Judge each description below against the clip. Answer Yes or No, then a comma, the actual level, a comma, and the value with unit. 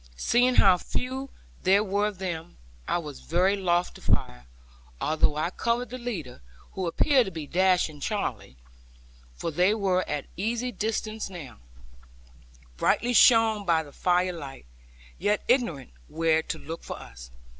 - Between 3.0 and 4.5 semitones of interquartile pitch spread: No, average, 5.3 semitones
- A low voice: No, medium, 185 Hz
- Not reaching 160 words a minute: Yes, average, 150 wpm